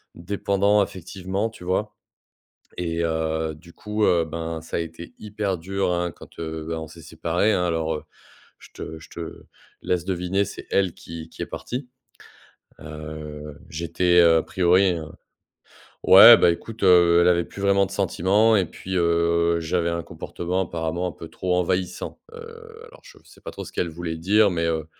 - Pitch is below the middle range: Yes, very low, 85 Hz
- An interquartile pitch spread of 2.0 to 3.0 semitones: Yes, narrow, 2.5 semitones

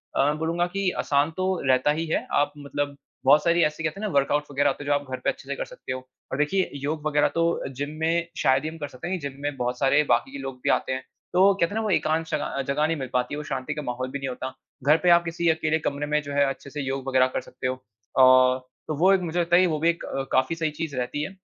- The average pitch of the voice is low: No, medium, 150 Hz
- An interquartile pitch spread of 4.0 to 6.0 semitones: No, average, 3.4 semitones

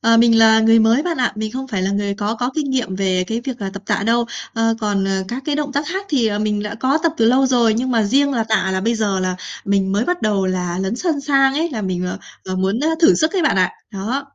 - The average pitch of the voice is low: No, high, 225 Hz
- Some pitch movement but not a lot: Yes, average, 5.0 semitones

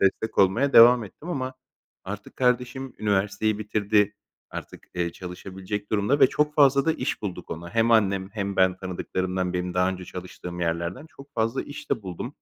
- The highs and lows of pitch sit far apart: No, average, 4.8 semitones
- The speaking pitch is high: No, low, 105 Hz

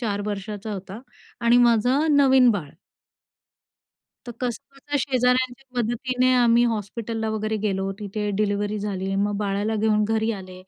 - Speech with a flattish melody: No, average, 3.3 semitones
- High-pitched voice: Yes, high, 220 Hz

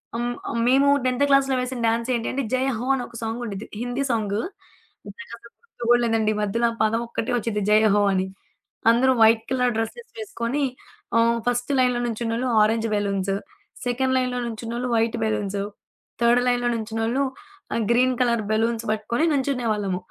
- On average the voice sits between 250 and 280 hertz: No, high, 235 Hz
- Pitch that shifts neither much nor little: No, narrow, 2.1 semitones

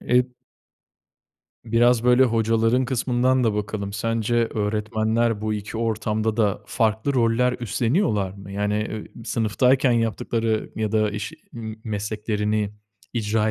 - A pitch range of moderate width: No, narrow, 1.8 semitones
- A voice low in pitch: Yes, low, 110 Hz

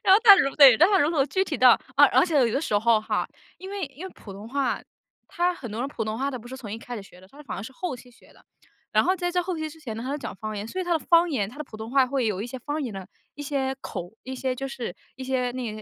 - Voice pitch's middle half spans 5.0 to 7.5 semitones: Yes, wide, 5.5 semitones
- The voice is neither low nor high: No, very high, 265 Hz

